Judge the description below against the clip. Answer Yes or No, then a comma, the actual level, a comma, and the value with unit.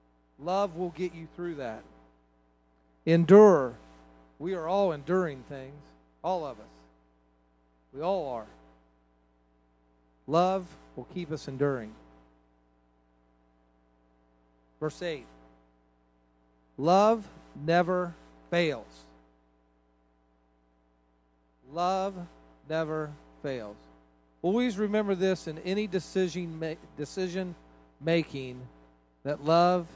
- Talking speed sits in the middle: No, slow, 80 wpm